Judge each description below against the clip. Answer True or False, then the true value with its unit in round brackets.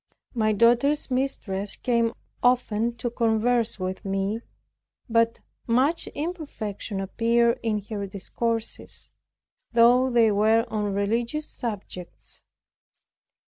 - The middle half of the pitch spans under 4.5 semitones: True (2.6 semitones)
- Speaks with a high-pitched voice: True (230 Hz)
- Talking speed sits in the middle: False (100 wpm)